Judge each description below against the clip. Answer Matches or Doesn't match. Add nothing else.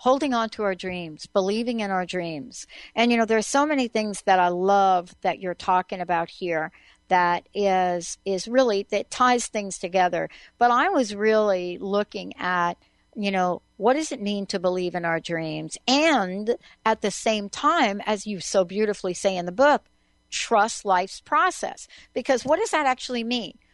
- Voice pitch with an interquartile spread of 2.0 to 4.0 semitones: Doesn't match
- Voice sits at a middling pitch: Doesn't match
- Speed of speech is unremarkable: Matches